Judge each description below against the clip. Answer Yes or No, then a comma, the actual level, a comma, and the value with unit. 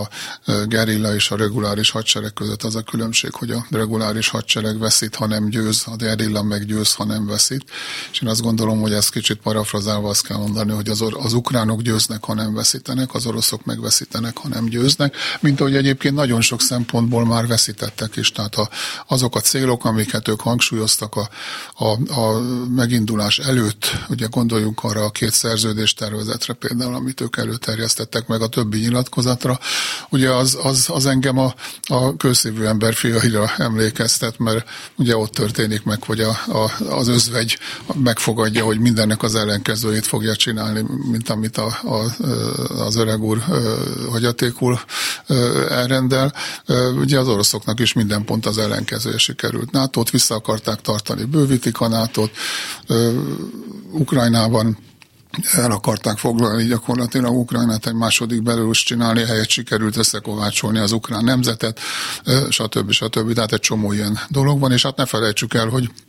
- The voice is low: Yes, low, 115 Hz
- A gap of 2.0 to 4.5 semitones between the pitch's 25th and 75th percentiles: Yes, narrow, 2.4 semitones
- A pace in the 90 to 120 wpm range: No, fast, 155 wpm